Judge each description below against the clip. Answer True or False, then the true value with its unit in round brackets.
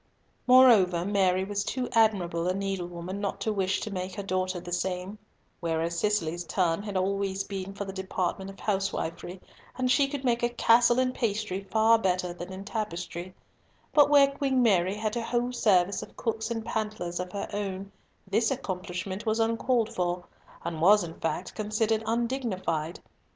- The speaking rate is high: False (170 wpm)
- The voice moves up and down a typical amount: True (3.7 semitones)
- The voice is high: True (195 Hz)